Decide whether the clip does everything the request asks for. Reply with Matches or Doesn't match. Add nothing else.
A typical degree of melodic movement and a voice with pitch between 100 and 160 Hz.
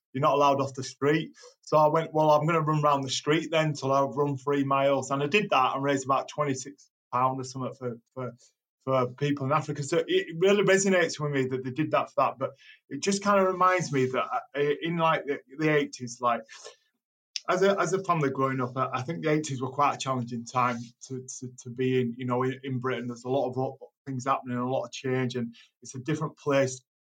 Matches